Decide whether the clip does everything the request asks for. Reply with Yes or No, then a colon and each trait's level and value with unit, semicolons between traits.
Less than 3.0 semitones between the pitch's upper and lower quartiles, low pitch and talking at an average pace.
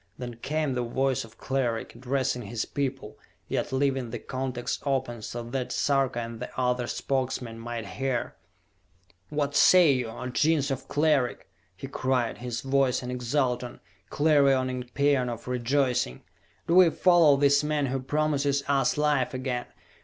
Yes: narrow, 2.5 semitones; low, 130 Hz; average, 150 wpm